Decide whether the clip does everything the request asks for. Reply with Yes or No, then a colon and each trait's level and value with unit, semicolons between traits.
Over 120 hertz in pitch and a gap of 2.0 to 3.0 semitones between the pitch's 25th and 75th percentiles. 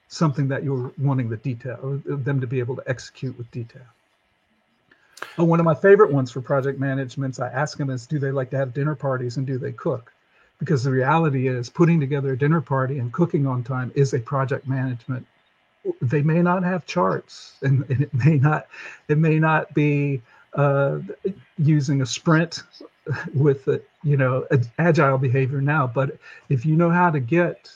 Yes: medium, 140 Hz; narrow, 2.6 semitones